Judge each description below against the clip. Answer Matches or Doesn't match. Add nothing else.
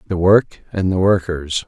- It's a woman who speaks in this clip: Doesn't match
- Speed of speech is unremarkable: Matches